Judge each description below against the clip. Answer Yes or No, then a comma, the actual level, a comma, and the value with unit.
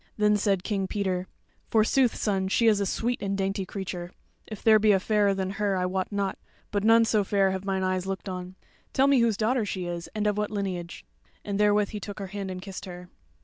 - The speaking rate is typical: No, fast, 230 wpm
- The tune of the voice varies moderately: No, narrow, 1.9 semitones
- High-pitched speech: Yes, high, 200 Hz